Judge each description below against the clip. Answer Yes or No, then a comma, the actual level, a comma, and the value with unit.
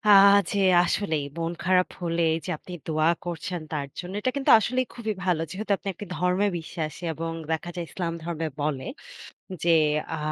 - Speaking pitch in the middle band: Yes, medium, 175 Hz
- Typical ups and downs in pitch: Yes, average, 3.5 semitones